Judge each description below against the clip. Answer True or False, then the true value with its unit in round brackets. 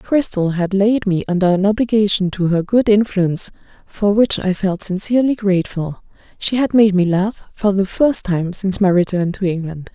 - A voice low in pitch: False (195 Hz)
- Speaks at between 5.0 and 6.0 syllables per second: True (5.1 syllables/s)